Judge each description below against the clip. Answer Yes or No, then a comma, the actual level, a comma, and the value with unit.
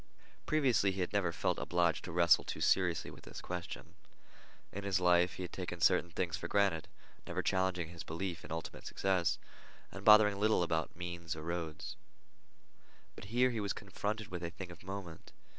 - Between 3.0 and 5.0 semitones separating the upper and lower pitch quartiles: No, narrow, 2.6 semitones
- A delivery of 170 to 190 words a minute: Yes, average, 180 wpm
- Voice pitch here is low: Yes, very low, 90 Hz